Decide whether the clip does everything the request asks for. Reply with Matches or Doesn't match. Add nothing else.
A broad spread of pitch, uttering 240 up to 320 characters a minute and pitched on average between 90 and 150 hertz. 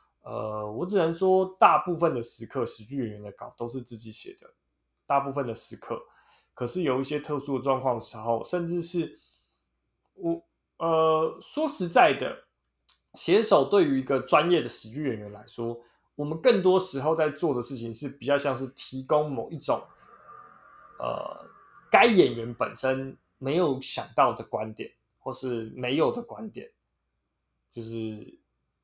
Doesn't match